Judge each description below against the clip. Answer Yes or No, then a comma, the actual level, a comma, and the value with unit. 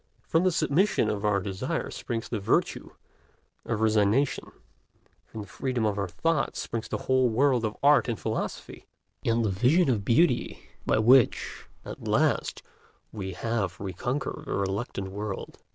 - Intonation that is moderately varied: Yes, average, 4.6 semitones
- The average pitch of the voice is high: No, low, 115 Hz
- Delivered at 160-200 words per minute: No, average, 150 wpm